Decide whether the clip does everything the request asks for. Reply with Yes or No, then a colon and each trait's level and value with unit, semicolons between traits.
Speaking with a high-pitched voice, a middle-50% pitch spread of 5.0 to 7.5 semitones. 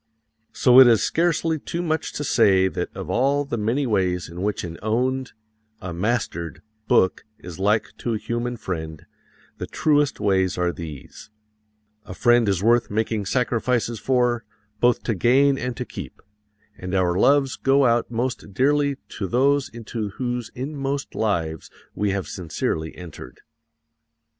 No: low, 115 Hz; wide, 5.5 semitones